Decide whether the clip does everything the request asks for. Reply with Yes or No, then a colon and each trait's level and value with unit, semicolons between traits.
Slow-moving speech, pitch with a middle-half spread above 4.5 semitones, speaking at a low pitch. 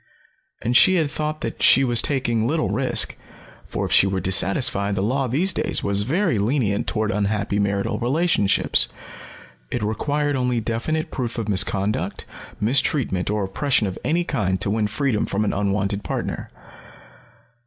No: average, 155 wpm; average, 5.3 semitones; low, 110 Hz